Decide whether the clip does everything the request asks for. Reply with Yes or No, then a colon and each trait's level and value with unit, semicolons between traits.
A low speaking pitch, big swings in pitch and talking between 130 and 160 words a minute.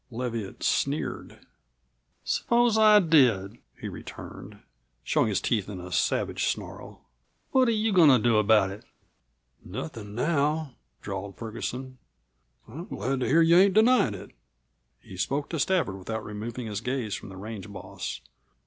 Yes: low, 120 Hz; wide, 7.9 semitones; average, 150 wpm